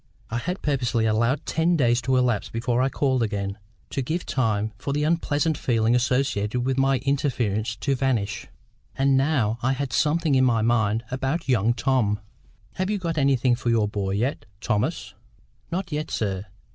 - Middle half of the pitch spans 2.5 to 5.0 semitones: Yes, average, 3.8 semitones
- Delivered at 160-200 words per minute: Yes, average, 170 wpm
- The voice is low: Yes, low, 125 Hz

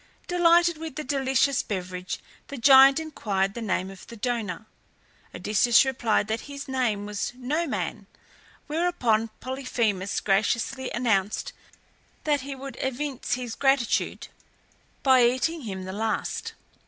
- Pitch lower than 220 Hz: No, very high, 250 Hz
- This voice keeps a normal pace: No, slow, 125 wpm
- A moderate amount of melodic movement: Yes, average, 4.6 semitones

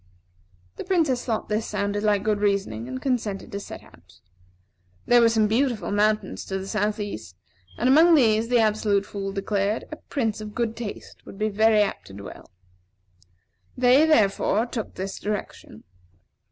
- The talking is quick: No, average, 165 wpm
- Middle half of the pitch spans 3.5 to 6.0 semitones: No, average, 2.7 semitones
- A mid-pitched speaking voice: No, high, 215 Hz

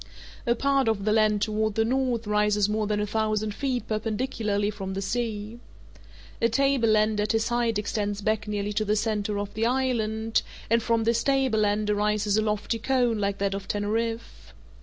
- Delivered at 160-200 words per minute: Yes, average, 180 wpm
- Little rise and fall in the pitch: Yes, narrow, 1.8 semitones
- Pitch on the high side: Yes, high, 215 Hz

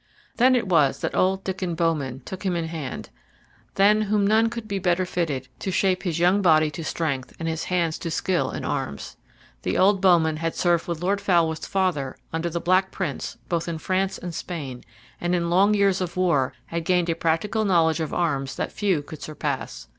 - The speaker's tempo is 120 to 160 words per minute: No, average, 200 wpm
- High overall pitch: No, medium, 175 Hz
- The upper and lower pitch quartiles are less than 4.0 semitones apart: Yes, average, 3.0 semitones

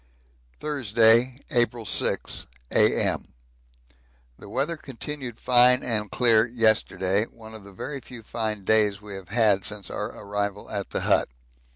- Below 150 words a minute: Yes, average, 140 wpm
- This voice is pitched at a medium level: No, low, 110 Hz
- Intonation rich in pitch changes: No, average, 3.2 semitones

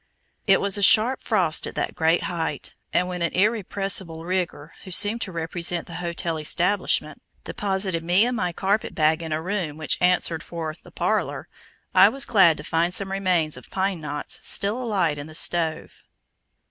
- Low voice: No, medium, 180 Hz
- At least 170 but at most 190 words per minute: Yes, average, 175 wpm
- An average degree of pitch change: Yes, average, 3.2 semitones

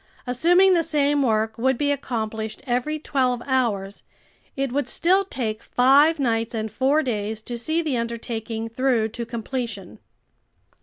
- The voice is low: No, high, 245 Hz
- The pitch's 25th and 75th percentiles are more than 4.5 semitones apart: No, average, 4.1 semitones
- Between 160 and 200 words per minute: No, average, 145 wpm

